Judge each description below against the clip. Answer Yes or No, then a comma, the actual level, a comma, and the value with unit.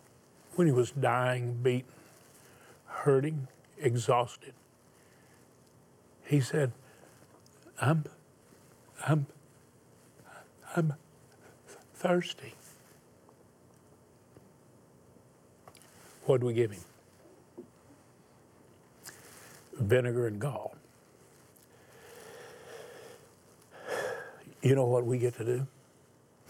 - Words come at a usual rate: No, slow, 65 wpm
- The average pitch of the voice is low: Yes, low, 125 Hz